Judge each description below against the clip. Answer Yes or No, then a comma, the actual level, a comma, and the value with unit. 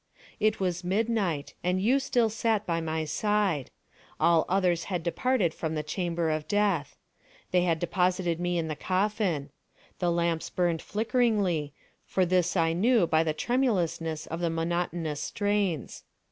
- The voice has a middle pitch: Yes, medium, 175 Hz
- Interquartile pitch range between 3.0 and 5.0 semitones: Yes, average, 3.8 semitones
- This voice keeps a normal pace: Yes, average, 150 wpm